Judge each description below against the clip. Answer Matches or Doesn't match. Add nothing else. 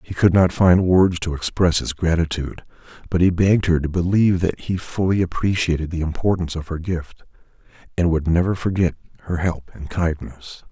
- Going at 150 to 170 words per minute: Doesn't match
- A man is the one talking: Matches